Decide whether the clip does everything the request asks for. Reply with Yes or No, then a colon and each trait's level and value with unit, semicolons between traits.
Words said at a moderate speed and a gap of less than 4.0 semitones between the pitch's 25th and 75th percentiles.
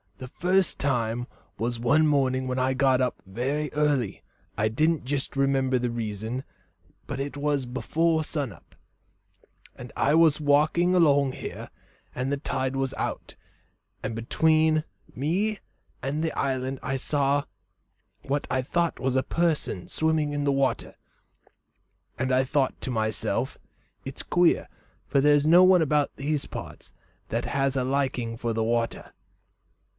Yes: average, 150 wpm; average, 2.8 semitones